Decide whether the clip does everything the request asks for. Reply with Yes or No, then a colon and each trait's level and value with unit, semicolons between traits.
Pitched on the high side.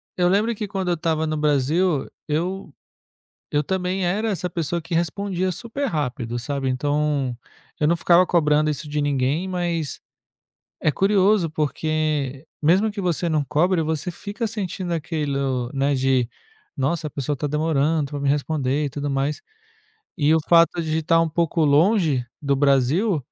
No: medium, 155 Hz